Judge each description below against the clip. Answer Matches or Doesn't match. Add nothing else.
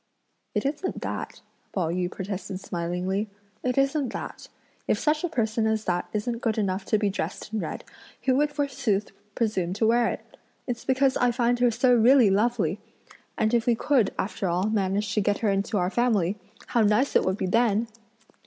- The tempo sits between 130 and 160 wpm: Doesn't match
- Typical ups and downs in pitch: Matches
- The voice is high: Matches